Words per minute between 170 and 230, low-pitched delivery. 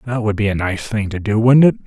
No: fast, 320 wpm; low, 110 Hz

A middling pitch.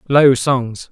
No: low, 130 Hz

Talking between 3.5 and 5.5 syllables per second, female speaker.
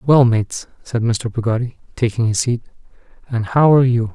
No: 5.4 syllables/s; male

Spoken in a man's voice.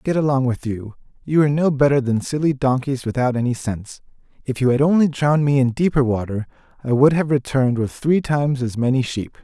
Yes: male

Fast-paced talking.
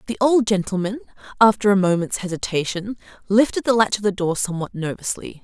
No: average, 165 wpm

